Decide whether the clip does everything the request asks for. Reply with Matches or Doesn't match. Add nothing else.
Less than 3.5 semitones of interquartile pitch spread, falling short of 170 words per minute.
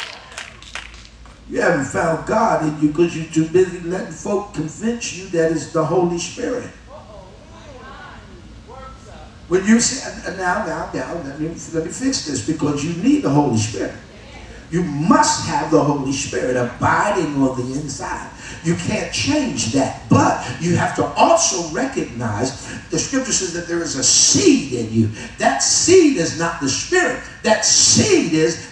Doesn't match